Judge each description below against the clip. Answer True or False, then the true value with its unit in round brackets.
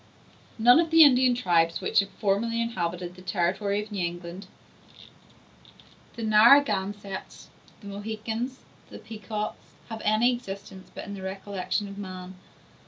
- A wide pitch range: False (3.3 semitones)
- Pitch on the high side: True (205 Hz)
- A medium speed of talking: False (120 wpm)